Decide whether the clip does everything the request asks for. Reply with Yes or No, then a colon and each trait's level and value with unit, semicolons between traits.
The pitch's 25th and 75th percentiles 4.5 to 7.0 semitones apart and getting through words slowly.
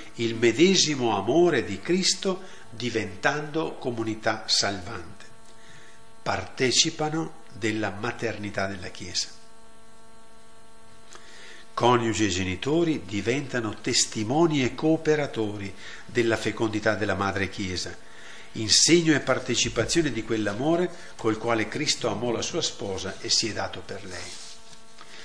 Yes: average, 5.1 semitones; slow, 100 wpm